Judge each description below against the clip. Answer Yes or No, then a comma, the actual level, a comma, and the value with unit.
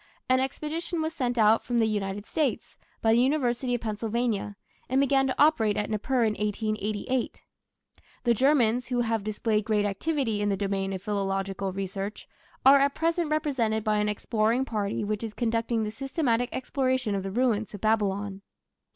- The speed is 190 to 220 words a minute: No, average, 170 wpm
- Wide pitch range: No, average, 3.9 semitones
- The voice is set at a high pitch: Yes, high, 225 Hz